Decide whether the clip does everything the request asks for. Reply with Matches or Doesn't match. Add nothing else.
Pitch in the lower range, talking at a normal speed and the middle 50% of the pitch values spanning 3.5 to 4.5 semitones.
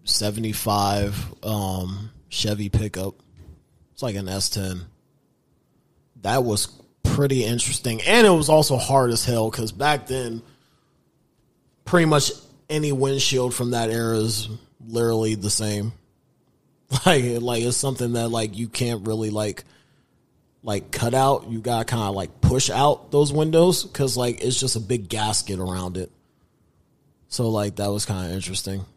Matches